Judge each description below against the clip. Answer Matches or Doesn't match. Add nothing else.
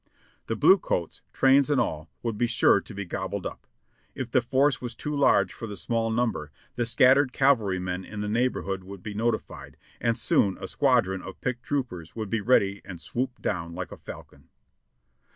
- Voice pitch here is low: Matches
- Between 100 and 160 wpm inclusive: Doesn't match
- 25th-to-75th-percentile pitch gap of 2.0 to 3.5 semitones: Doesn't match